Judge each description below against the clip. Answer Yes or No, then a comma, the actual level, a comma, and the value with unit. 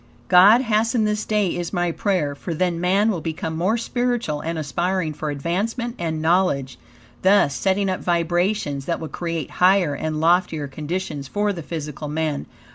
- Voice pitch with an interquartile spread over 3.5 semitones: Yes, average, 4.2 semitones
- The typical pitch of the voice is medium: Yes, medium, 175 Hz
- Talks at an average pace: Yes, average, 165 wpm